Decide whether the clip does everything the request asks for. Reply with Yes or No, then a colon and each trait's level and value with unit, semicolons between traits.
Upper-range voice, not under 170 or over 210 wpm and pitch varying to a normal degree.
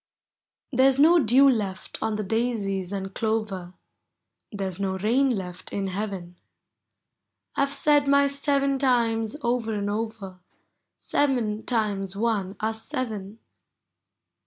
No: high, 220 Hz; slow, 135 wpm; average, 4.7 semitones